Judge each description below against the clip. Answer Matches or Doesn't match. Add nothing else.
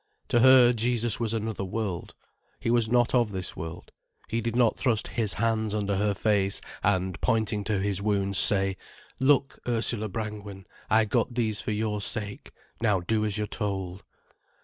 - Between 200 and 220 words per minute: Doesn't match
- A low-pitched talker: Matches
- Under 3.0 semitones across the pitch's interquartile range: Matches